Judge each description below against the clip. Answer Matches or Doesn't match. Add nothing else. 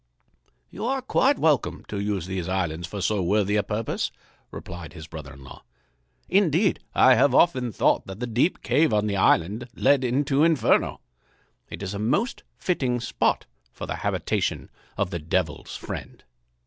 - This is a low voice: Matches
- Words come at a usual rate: Matches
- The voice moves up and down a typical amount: Doesn't match